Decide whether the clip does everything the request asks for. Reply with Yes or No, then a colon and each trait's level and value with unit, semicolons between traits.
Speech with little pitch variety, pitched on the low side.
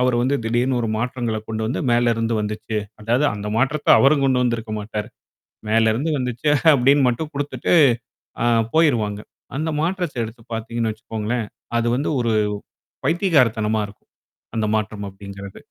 No: average, 3.5 semitones; low, 120 Hz